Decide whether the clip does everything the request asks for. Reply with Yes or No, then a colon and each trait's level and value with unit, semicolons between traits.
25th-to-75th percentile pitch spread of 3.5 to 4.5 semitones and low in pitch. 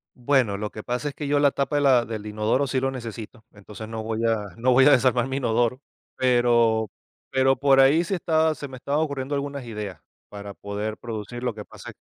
Yes: average, 3.9 semitones; low, 125 Hz